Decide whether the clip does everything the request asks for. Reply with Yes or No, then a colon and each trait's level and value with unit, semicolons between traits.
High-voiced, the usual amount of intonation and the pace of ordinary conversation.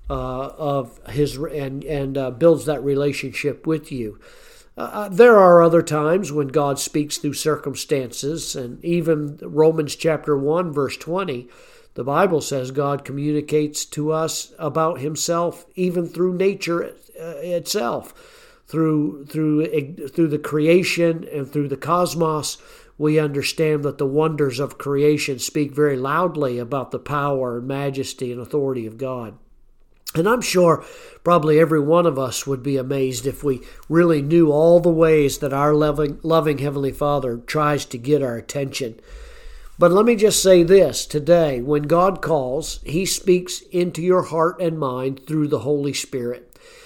No: medium, 150 Hz; average, 3.4 semitones; average, 150 wpm